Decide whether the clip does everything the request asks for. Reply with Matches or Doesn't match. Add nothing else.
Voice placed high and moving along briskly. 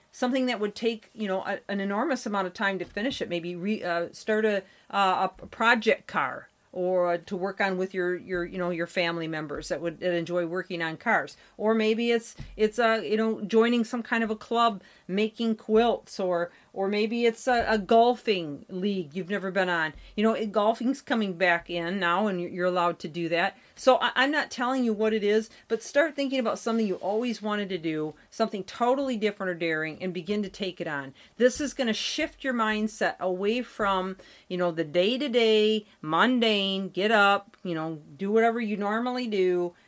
Matches